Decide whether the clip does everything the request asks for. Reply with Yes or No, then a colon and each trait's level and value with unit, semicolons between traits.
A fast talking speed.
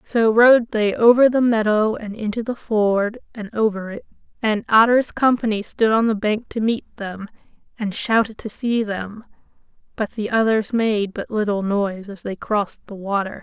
No: average, 180 wpm